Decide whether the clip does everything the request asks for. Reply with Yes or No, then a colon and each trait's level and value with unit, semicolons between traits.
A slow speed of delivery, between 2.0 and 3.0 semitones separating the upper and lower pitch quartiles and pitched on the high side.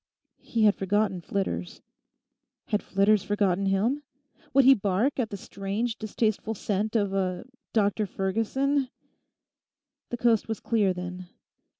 Yes: slow, 120 wpm; average, 2.7 semitones; high, 205 Hz